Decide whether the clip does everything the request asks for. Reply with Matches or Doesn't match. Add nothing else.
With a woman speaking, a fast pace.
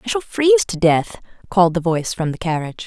Matches